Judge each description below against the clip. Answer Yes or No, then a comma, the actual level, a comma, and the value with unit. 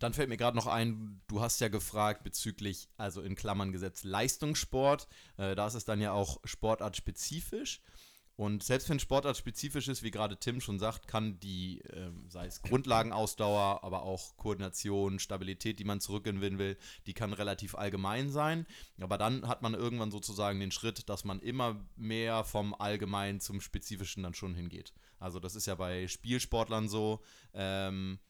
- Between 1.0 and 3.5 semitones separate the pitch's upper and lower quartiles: Yes, average, 2.8 semitones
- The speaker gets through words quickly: No, average, 175 wpm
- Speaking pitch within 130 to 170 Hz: No, low, 105 Hz